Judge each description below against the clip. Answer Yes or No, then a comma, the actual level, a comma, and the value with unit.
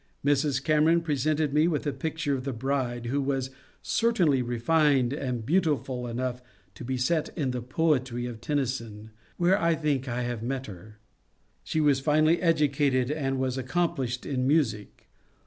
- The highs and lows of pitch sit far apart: No, average, 3.7 semitones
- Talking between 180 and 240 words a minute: No, average, 160 wpm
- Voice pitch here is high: No, low, 135 Hz